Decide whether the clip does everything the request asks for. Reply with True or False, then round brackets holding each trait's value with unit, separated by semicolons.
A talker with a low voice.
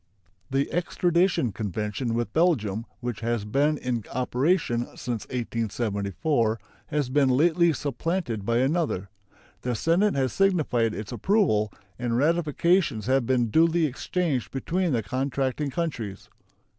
True (130 Hz)